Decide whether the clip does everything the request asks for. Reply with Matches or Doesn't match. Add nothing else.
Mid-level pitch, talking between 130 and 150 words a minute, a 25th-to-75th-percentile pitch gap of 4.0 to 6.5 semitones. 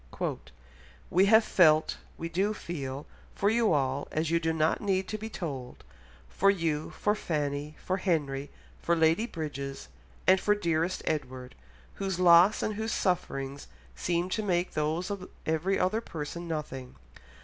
Matches